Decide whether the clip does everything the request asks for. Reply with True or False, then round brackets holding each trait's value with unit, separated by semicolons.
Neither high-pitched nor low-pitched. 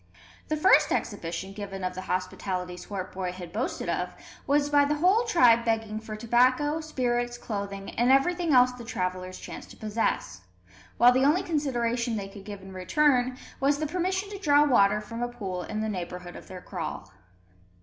False (235 Hz)